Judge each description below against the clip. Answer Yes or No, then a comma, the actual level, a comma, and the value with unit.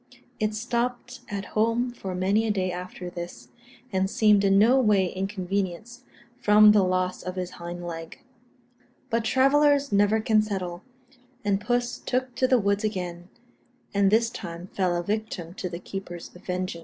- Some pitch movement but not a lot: Yes, average, 3.4 semitones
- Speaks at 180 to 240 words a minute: No, average, 160 wpm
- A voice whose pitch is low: No, high, 200 Hz